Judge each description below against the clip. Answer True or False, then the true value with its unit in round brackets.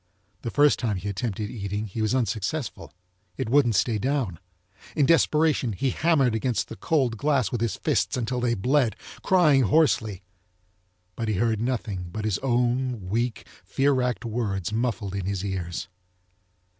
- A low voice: True (115 Hz)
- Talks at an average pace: True (155 wpm)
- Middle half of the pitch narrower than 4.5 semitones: True (4.1 semitones)